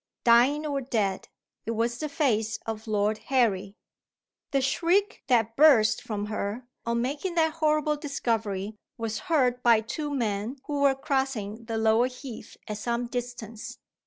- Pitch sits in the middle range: No, high, 240 Hz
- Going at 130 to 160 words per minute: Yes, average, 150 wpm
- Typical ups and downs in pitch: Yes, average, 4.2 semitones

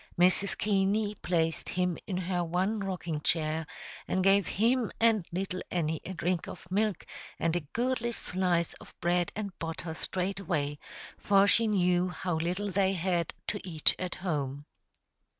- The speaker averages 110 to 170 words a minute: Yes, average, 150 wpm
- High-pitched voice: No, medium, 180 Hz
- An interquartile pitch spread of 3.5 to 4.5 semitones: No, average, 2.8 semitones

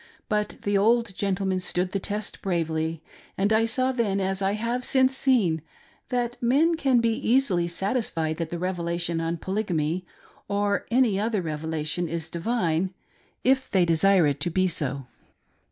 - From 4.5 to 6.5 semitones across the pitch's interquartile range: Yes, average, 5.3 semitones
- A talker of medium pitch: No, high, 195 Hz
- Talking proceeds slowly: No, average, 155 wpm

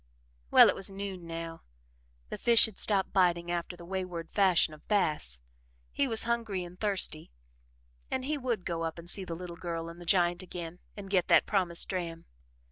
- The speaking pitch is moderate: Yes, medium, 180 Hz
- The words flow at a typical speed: Yes, average, 190 wpm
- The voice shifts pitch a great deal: No, average, 2.7 semitones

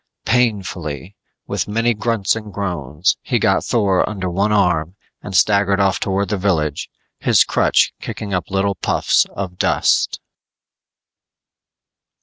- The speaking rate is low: Yes, slow, 130 wpm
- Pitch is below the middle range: Yes, low, 100 Hz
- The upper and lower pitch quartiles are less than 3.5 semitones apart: Yes, narrow, 2.6 semitones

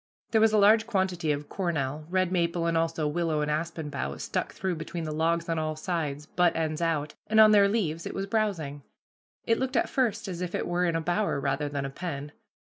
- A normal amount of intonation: Yes, average, 3.8 semitones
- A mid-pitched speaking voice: Yes, medium, 165 Hz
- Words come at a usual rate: No, fast, 225 wpm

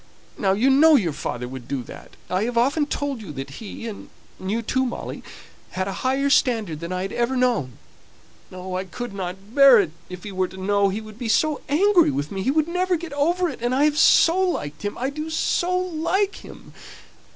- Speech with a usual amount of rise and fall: No, wide, 7.8 semitones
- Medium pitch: No, high, 235 Hz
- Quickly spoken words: Yes, fast, 215 wpm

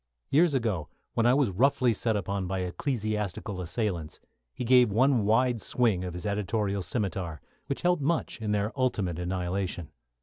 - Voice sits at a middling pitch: No, low, 105 Hz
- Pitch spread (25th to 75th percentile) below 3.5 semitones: No, average, 5.1 semitones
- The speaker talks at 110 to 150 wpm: No, average, 160 wpm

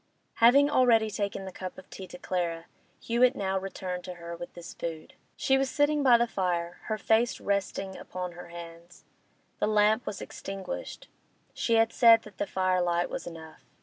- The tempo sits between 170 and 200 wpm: Yes, average, 180 wpm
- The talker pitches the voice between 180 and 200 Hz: Yes, high, 190 Hz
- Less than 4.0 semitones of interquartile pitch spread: No, average, 4.4 semitones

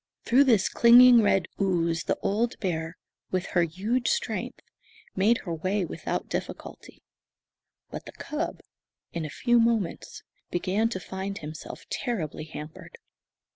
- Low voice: No, high, 190 Hz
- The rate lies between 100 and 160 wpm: Yes, slow, 135 wpm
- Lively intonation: Yes, wide, 5.7 semitones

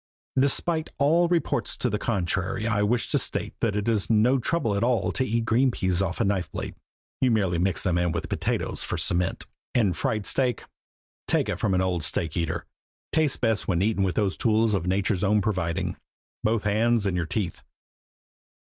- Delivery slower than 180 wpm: No, average, 195 wpm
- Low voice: Yes, low, 105 Hz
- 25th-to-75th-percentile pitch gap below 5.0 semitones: Yes, average, 4.1 semitones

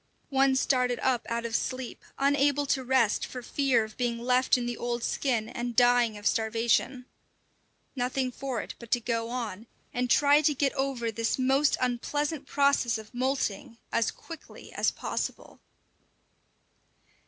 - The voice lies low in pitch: No, very high, 250 Hz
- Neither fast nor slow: Yes, average, 155 wpm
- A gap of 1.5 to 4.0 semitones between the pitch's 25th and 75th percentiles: Yes, narrow, 2.4 semitones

